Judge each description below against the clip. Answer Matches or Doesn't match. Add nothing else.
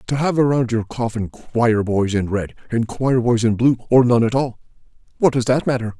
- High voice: Doesn't match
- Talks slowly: Doesn't match